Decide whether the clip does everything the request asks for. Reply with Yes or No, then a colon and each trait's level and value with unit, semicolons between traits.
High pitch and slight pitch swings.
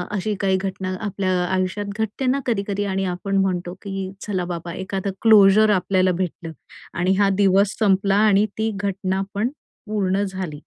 Yes: high, 195 Hz; narrow, 1.6 semitones